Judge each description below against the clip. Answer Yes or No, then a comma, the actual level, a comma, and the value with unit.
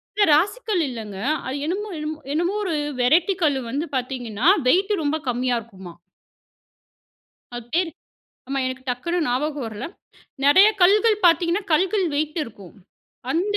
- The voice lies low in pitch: No, very high, 305 Hz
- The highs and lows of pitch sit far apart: Yes, wide, 6.7 semitones